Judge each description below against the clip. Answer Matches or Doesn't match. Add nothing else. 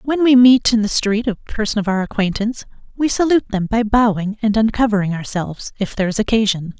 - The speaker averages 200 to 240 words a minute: Matches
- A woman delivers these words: Matches